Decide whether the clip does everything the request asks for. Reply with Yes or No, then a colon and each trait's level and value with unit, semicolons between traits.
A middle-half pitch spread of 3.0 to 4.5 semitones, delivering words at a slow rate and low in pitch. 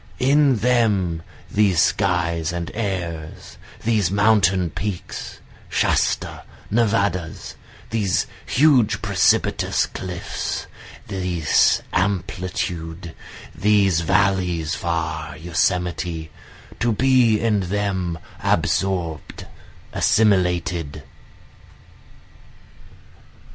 Yes: average, 3.7 semitones; slow, 70 wpm; very low, 95 Hz